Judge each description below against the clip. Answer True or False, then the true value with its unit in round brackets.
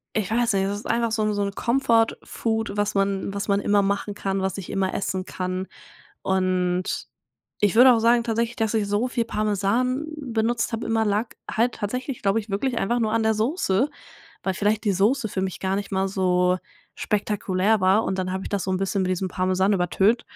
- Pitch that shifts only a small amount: False (3.0 semitones)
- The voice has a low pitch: False (205 Hz)